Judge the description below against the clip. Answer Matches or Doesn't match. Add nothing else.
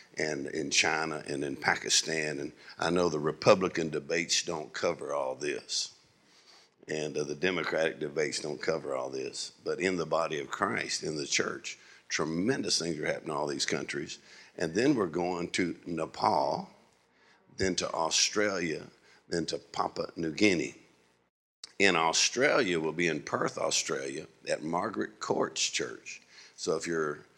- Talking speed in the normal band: Matches